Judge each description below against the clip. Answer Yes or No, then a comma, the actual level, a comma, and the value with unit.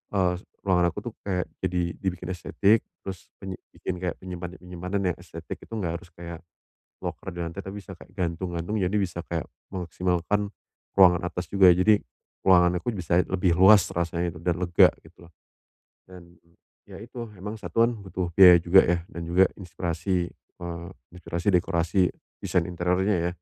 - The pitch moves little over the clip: Yes, narrow, 1.7 semitones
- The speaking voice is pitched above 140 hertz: No, very low, 90 Hz